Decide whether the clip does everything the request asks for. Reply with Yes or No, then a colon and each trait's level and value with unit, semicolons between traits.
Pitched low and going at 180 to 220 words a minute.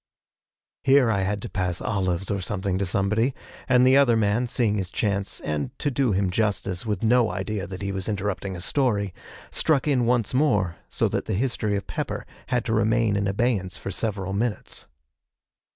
Yes: low, 105 Hz; average, 185 wpm